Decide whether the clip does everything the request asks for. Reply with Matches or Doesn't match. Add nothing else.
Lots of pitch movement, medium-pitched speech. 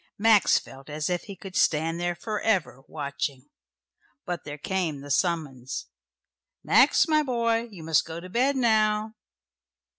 Matches